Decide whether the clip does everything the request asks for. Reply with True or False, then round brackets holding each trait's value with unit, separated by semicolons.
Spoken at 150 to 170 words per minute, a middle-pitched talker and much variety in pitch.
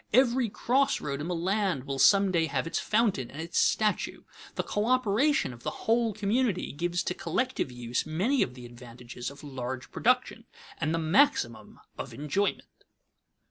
True (165 wpm; 170 Hz; 8.3 semitones)